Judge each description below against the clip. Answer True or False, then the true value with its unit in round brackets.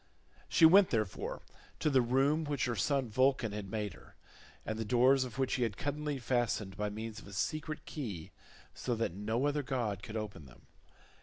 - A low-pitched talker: True (120 Hz)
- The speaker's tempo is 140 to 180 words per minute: False (190 wpm)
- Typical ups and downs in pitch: True (4.6 semitones)